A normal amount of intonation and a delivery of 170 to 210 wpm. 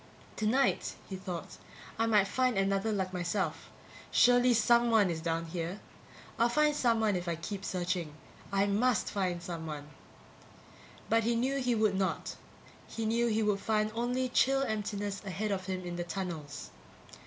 No: average, 4.2 semitones; average, 155 wpm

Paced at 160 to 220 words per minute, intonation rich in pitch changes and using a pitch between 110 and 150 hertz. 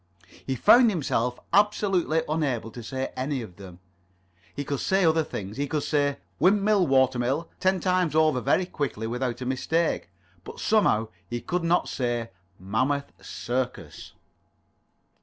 No: average, 145 wpm; wide, 5.7 semitones; medium, 140 Hz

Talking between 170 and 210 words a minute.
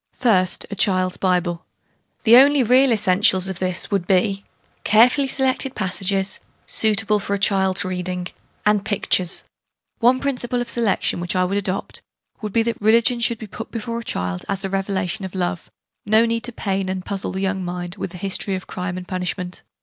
Yes: average, 185 wpm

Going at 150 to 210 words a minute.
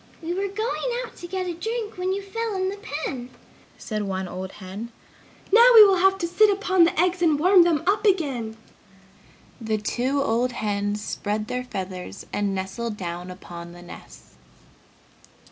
Yes: average, 175 wpm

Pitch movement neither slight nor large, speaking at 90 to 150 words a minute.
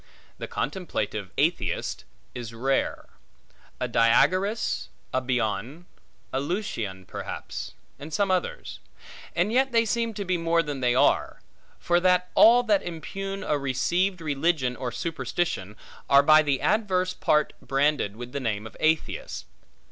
No: wide, 6.7 semitones; average, 140 wpm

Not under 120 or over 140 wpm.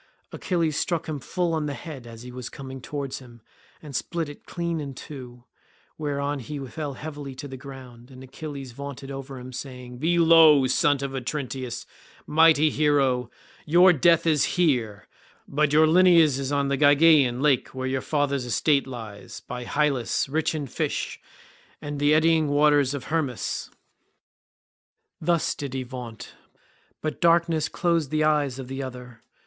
No: average, 165 wpm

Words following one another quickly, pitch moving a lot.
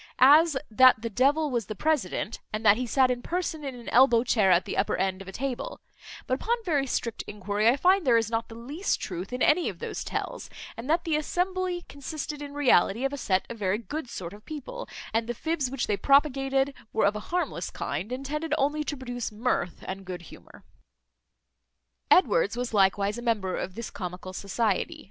Yes: fast, 210 wpm; wide, 5.8 semitones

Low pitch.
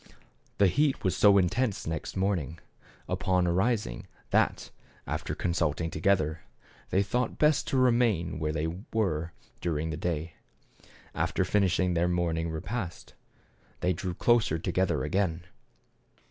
Yes: very low, 90 Hz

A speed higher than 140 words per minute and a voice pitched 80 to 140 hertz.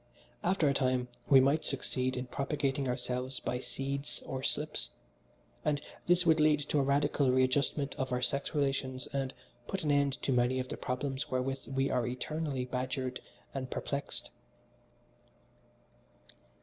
Yes: average, 150 wpm; low, 135 Hz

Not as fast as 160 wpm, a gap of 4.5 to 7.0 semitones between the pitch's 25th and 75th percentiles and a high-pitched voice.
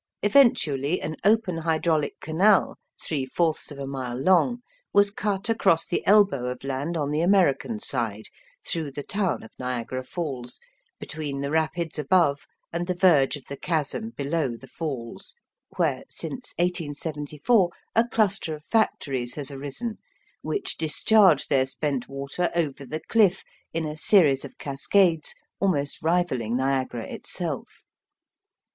No: average, 140 wpm; average, 5.1 semitones; medium, 155 Hz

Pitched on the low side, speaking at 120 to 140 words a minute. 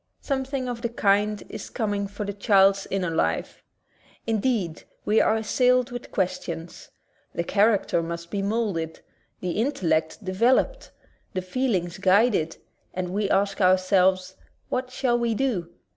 No: high, 200 Hz; slow, 135 wpm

